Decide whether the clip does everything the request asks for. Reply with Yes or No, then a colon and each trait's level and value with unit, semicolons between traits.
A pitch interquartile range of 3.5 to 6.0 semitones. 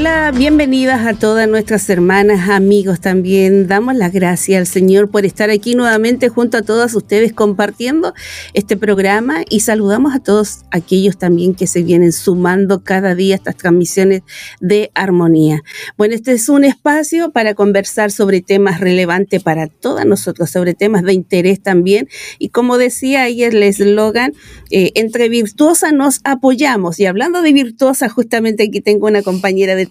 Yes: average, 4.0 semitones